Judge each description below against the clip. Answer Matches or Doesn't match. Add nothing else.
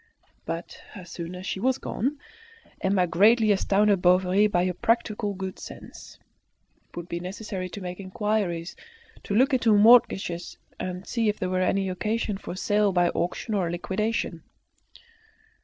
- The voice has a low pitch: Doesn't match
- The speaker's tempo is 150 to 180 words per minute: Matches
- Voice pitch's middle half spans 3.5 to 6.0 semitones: Doesn't match